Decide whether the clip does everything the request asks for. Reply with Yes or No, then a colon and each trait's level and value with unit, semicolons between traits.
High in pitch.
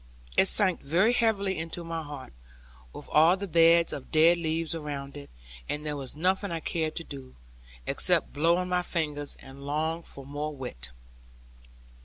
No: medium, 160 Hz